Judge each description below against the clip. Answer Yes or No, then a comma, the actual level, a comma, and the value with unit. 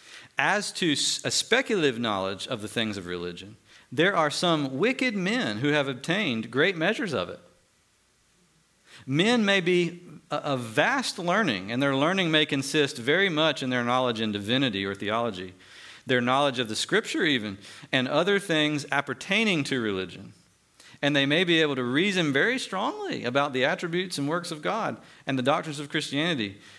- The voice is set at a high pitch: No, medium, 140 Hz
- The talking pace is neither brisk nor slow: Yes, average, 170 wpm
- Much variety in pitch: Yes, wide, 5.8 semitones